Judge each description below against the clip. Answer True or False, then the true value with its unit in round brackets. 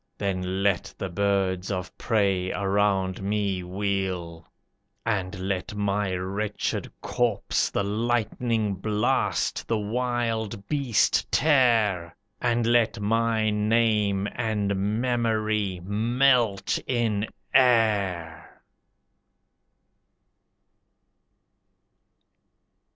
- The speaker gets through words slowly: True (80 wpm)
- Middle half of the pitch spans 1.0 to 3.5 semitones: True (3.0 semitones)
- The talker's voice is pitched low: True (105 Hz)